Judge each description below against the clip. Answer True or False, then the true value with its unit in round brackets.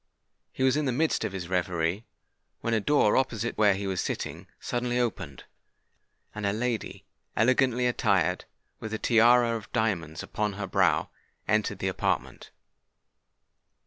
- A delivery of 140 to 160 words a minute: True (150 wpm)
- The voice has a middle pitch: False (110 Hz)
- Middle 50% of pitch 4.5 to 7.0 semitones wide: False (3.8 semitones)